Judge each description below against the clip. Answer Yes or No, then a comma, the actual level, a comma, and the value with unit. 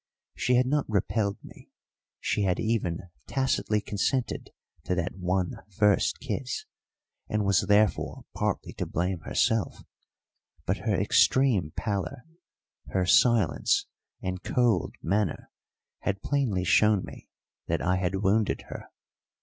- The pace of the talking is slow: Yes, slow, 125 wpm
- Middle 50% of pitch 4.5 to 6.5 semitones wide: No, average, 3.6 semitones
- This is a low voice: Yes, low, 100 Hz